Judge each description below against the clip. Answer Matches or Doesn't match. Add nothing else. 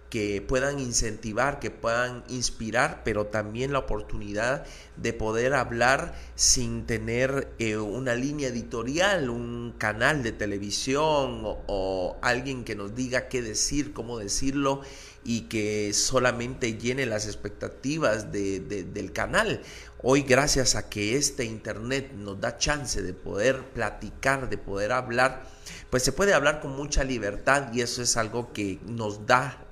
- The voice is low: Matches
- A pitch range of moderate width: Matches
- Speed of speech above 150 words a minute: Doesn't match